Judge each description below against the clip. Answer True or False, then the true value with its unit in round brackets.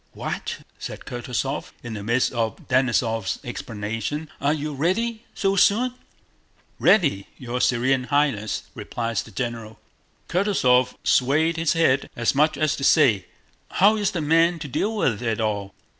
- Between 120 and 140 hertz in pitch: True (135 Hz)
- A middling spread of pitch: False (5.7 semitones)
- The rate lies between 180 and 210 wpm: False (145 wpm)